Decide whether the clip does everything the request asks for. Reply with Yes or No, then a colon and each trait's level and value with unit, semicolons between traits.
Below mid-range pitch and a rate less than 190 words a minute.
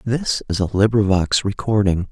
Yes: low, 105 Hz; average, 140 wpm